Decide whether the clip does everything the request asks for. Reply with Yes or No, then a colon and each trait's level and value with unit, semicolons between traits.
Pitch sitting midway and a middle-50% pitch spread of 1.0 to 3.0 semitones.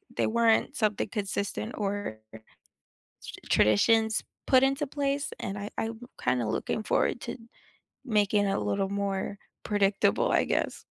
No: high, 205 Hz; narrow, 2.5 semitones